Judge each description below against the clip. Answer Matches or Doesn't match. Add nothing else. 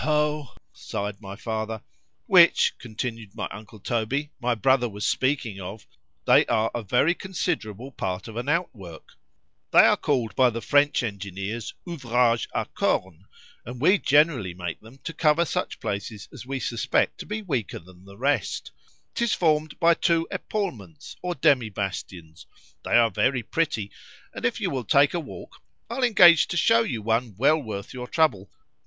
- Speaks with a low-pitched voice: Matches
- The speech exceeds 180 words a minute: Doesn't match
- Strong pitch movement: Matches